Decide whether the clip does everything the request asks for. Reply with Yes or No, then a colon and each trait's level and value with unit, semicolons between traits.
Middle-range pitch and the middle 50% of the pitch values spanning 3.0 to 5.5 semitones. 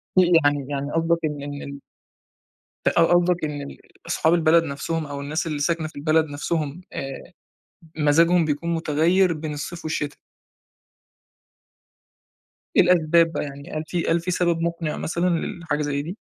No: medium, 160 Hz; narrow, 2.6 semitones